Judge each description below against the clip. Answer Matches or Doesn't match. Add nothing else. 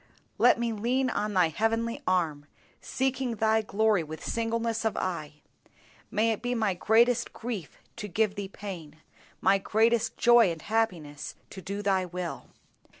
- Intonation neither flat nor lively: Matches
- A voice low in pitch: Doesn't match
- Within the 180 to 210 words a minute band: Doesn't match